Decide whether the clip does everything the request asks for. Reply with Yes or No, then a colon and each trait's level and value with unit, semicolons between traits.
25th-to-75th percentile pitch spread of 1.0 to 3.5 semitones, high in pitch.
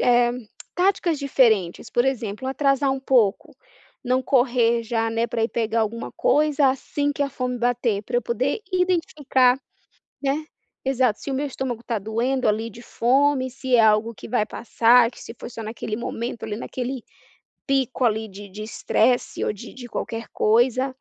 Yes: average, 2.8 semitones; high, 245 Hz